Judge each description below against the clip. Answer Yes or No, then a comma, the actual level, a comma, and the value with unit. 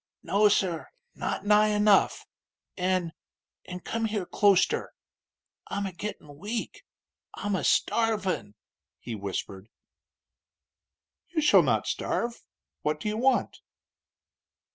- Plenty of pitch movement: No, average, 3.6 semitones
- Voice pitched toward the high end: Yes, high, 200 Hz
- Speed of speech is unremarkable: No, slow, 110 wpm